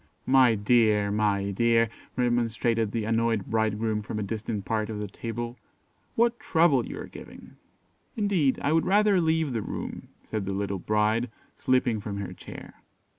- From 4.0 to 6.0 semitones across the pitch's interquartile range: No, average, 3.3 semitones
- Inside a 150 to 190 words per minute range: Yes, average, 160 wpm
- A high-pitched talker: No, low, 115 Hz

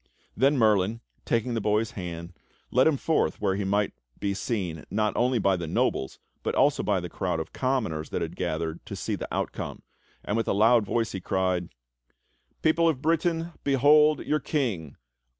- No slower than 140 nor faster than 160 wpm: No, average, 180 wpm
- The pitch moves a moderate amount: No, wide, 6.3 semitones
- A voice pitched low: Yes, low, 110 Hz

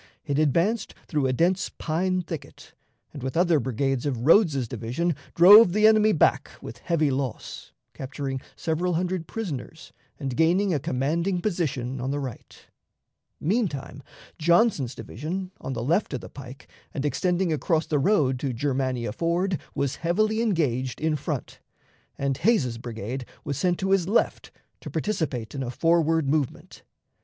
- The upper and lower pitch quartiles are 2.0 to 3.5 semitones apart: No, average, 5.2 semitones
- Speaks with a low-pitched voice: No, medium, 155 Hz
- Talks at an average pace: Yes, average, 150 wpm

